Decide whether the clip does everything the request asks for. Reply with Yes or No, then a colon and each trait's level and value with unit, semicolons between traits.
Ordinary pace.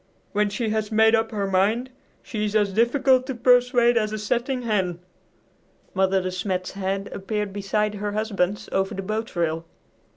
Yes: average, 170 wpm